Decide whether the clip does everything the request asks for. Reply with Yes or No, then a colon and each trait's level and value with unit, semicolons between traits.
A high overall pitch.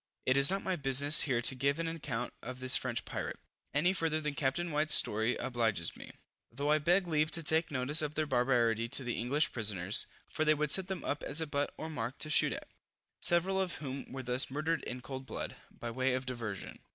No: medium, 140 Hz